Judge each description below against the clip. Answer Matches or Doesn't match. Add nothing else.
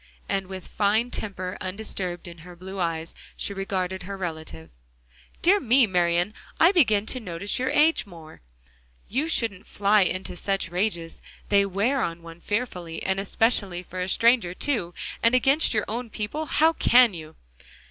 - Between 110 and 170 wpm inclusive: Matches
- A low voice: Doesn't match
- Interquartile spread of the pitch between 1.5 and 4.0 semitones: Doesn't match